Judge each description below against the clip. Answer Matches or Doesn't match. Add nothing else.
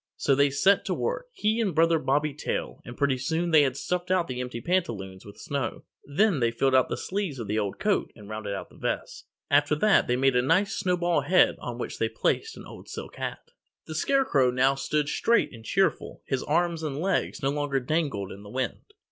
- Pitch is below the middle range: Doesn't match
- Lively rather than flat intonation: Matches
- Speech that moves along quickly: Matches